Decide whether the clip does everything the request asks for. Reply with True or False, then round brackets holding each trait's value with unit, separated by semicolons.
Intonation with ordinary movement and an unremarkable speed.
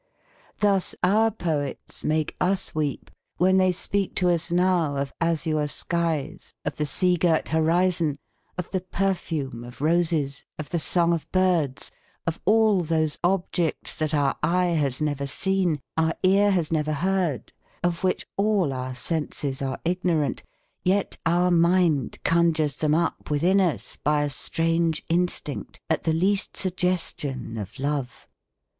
True (3.5 semitones; 145 wpm)